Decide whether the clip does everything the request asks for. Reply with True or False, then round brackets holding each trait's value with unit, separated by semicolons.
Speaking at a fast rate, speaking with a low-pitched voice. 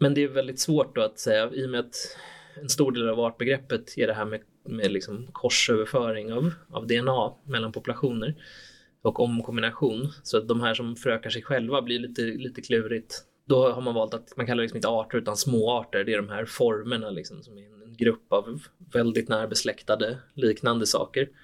True (200 wpm; 120 Hz)